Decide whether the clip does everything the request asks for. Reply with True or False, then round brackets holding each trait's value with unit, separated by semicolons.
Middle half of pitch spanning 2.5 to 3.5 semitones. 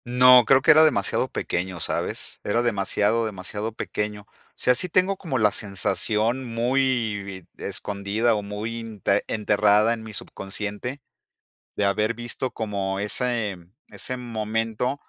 True (3.1 semitones)